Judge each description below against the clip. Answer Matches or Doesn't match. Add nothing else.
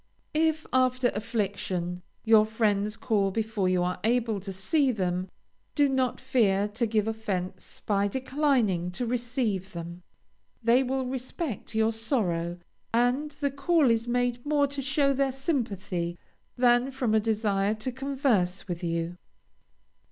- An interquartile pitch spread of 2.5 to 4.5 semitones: Doesn't match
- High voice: Matches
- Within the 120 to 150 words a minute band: Matches